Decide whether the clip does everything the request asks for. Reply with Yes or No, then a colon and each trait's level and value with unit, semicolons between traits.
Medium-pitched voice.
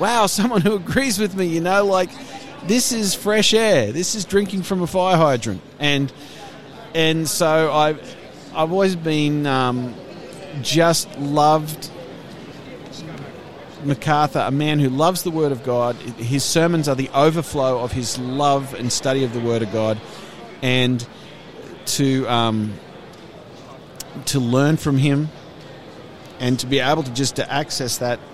Yes: medium, 150 Hz